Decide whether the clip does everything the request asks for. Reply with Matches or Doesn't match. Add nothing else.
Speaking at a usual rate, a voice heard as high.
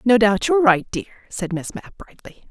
Doesn't match